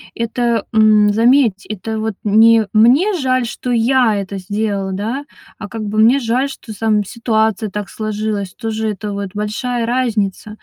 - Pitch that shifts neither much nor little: No, narrow, 2.2 semitones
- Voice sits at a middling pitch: No, high, 220 Hz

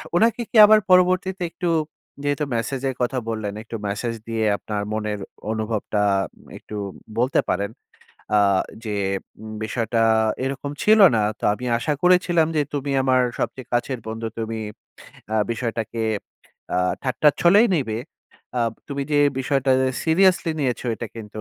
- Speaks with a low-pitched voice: Yes, low, 125 Hz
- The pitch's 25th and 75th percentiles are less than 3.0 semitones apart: No, wide, 5.4 semitones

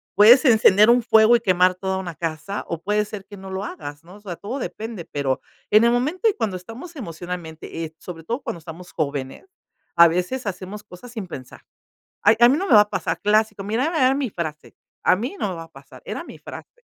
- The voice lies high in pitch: Yes, high, 200 Hz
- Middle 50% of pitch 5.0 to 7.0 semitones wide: Yes, wide, 5.5 semitones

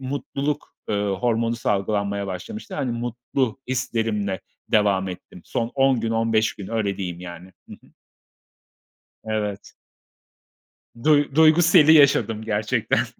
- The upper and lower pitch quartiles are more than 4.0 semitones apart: Yes, average, 4.5 semitones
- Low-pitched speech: Yes, low, 115 Hz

